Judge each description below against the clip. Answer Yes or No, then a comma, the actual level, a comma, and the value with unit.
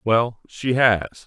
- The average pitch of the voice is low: Yes, low, 115 Hz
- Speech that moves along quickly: No, average, 140 wpm